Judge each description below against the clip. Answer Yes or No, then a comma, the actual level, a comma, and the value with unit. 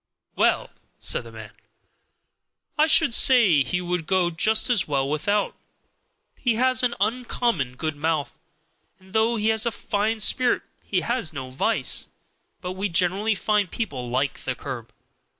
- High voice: Yes, high, 195 Hz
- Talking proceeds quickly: No, average, 150 wpm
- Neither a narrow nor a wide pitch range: No, wide, 6.7 semitones